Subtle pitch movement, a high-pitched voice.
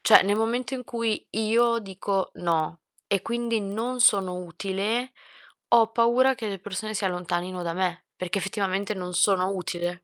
No: average, 3.9 semitones; high, 200 Hz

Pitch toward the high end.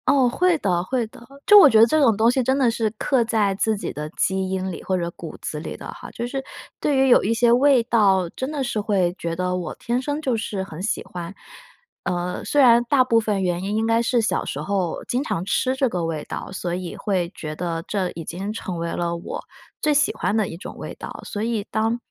Yes: high, 215 Hz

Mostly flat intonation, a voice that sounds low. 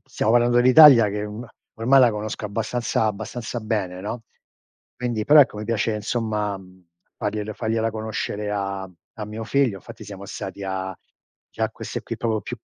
Yes: narrow, 2.3 semitones; low, 110 Hz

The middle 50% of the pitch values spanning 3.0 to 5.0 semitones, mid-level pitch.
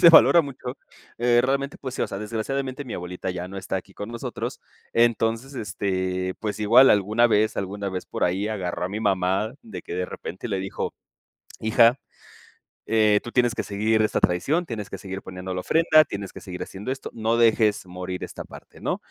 No: average, 4.1 semitones; low, 105 Hz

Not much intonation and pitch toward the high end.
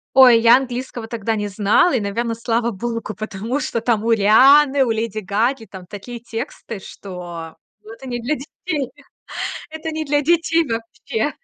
No: average, 3.7 semitones; high, 230 Hz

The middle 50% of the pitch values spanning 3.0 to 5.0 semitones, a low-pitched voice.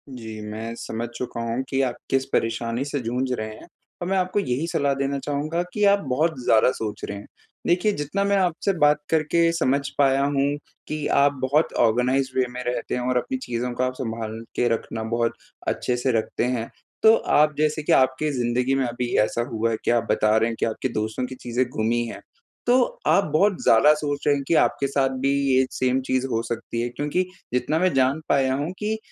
Yes: average, 4.1 semitones; low, 130 Hz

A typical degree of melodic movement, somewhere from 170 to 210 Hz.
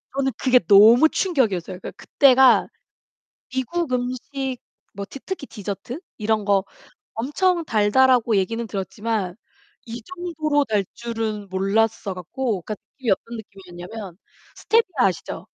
No: average, 4.7 semitones; high, 230 Hz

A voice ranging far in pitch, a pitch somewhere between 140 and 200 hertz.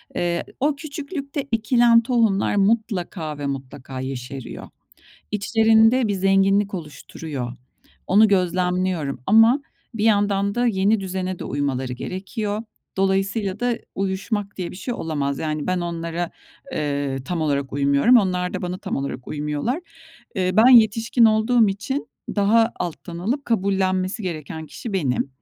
Yes: wide, 5.7 semitones; high, 190 Hz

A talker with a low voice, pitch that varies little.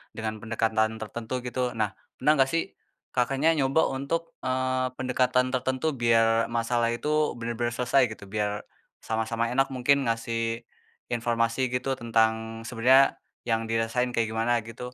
Yes: low, 120 Hz; narrow, 2.3 semitones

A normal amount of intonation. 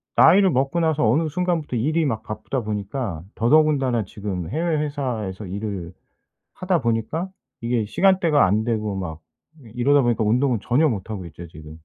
No: wide, 6.7 semitones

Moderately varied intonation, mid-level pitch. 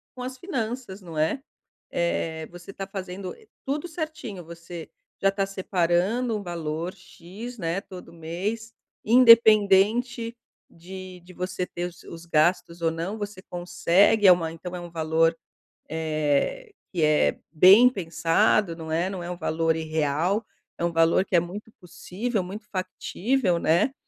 Yes: average, 4.1 semitones; medium, 180 Hz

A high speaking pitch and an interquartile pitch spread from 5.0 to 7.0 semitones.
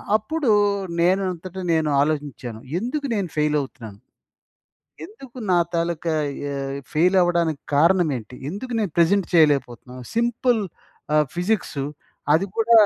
No: medium, 170 Hz; wide, 5.6 semitones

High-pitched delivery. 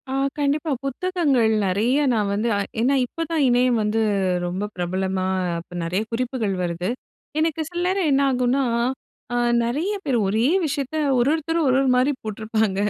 Yes: high, 245 Hz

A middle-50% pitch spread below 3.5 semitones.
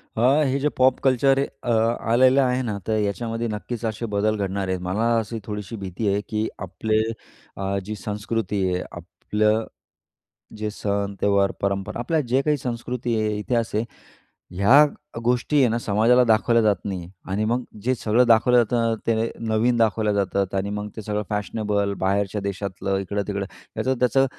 Yes: average, 2.8 semitones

